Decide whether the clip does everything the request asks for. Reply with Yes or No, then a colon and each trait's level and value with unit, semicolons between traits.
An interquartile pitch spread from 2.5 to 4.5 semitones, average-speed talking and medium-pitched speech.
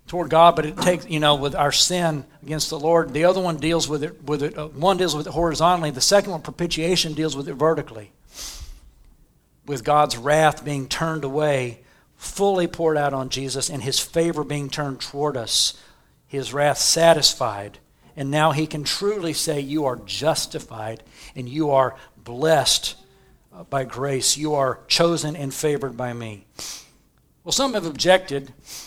Yes: average, 3.1 semitones; average, 170 wpm; medium, 150 Hz